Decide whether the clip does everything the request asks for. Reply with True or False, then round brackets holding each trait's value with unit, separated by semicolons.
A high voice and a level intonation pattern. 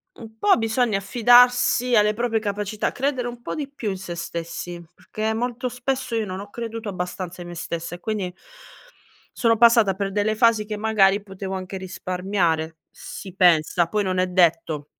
False (205 Hz; 3.9 semitones)